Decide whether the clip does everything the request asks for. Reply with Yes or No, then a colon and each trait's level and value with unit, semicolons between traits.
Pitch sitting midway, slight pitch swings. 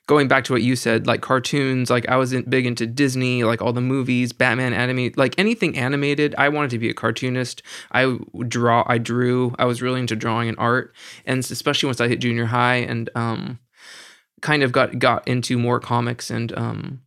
No: low, 125 Hz; narrow, 1.7 semitones